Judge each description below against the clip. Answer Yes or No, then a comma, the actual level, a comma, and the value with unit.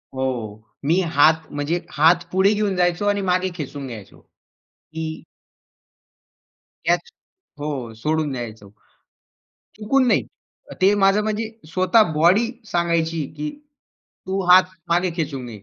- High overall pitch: No, medium, 165 Hz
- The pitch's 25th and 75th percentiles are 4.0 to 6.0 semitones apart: Yes, average, 4.8 semitones